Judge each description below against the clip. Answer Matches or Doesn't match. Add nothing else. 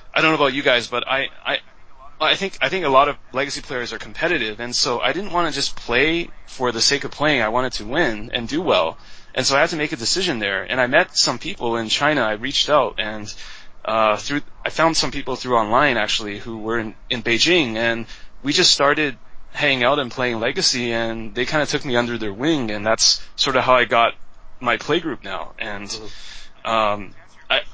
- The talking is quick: Matches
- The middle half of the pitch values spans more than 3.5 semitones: Matches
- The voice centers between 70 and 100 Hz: Doesn't match